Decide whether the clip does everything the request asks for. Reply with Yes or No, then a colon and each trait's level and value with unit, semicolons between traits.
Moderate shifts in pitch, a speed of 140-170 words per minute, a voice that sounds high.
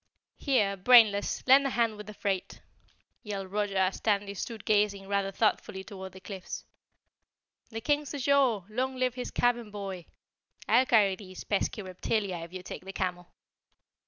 Yes: average, 3.6 semitones; average, 160 wpm; high, 205 Hz